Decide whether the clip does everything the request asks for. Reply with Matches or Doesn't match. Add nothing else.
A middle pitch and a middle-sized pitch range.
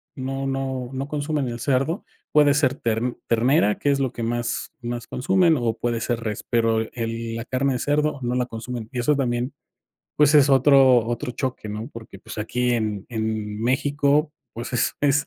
Doesn't match